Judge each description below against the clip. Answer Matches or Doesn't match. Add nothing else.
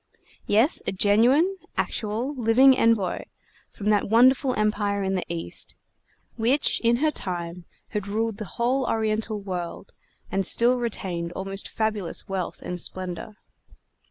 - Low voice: Doesn't match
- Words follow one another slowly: Matches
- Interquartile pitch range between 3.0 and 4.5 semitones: Matches